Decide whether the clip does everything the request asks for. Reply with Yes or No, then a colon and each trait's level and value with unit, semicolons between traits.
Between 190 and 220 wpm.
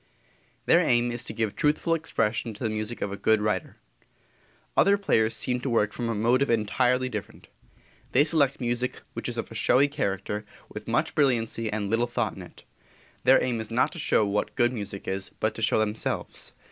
Yes: average, 195 wpm